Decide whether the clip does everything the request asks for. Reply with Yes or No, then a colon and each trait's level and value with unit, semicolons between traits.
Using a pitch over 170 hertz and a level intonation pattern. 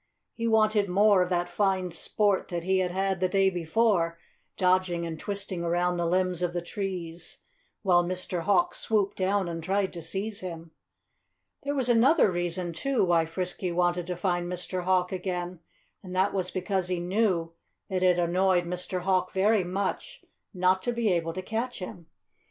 Yes: medium, 185 Hz; narrow, 1.8 semitones